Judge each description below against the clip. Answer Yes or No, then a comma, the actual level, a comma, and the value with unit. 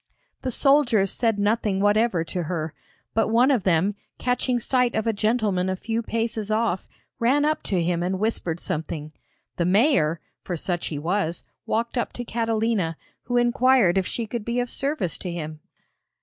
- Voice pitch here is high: Yes, high, 215 Hz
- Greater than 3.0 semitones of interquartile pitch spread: Yes, average, 4.9 semitones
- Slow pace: No, average, 175 wpm